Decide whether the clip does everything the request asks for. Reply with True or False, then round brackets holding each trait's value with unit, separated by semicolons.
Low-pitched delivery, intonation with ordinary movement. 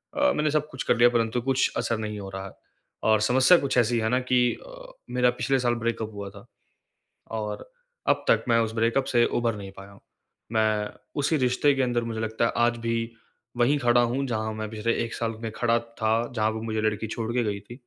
False (115 Hz; 2.2 semitones)